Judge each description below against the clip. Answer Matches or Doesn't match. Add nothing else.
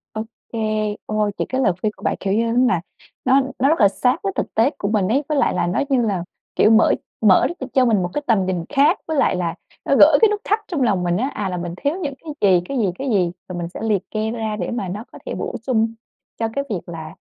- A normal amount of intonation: Doesn't match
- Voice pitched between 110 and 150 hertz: Doesn't match